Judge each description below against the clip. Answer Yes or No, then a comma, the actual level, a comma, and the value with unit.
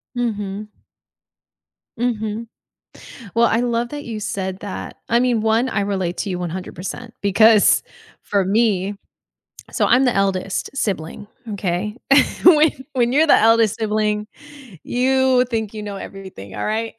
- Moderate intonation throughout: Yes, average, 3.2 semitones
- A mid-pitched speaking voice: No, high, 215 Hz